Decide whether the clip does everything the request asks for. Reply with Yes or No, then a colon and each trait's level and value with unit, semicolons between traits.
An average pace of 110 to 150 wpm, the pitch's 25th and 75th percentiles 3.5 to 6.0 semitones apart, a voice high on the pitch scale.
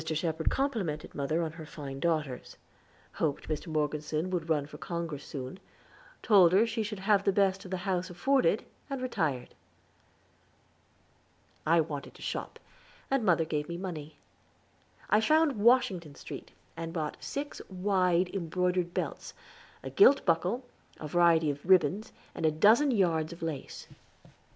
No: average, 145 wpm; average, 4.1 semitones; medium, 175 Hz